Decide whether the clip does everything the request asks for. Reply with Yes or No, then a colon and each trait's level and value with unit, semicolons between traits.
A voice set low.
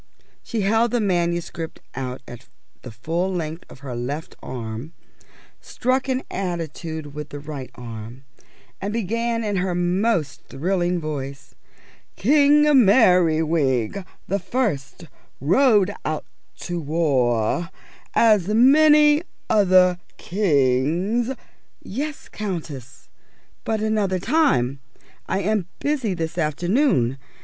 No: medium, 175 Hz